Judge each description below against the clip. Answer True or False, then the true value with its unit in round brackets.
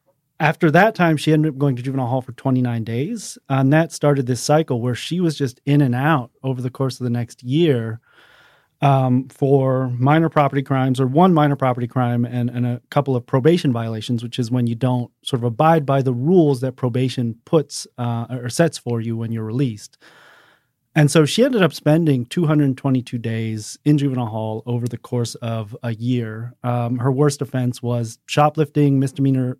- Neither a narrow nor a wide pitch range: True (3.5 semitones)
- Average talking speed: True (195 wpm)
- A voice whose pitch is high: False (130 Hz)